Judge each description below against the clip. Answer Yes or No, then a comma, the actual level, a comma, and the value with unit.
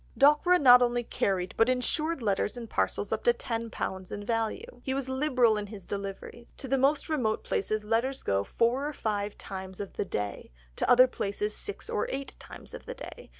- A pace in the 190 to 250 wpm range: Yes, average, 195 wpm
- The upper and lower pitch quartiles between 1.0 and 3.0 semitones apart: No, average, 4.8 semitones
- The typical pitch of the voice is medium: No, high, 235 Hz